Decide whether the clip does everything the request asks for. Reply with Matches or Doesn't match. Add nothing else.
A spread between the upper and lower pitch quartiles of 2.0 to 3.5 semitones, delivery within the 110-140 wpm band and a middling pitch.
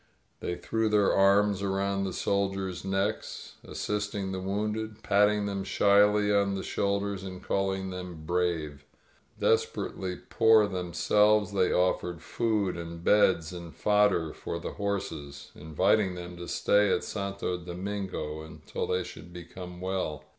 Doesn't match